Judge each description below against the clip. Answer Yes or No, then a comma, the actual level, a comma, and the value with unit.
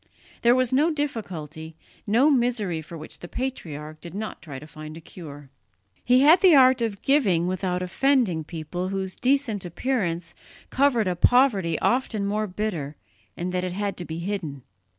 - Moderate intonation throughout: No, wide, 7.0 semitones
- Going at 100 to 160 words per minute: No, average, 170 wpm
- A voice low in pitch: No, high, 190 Hz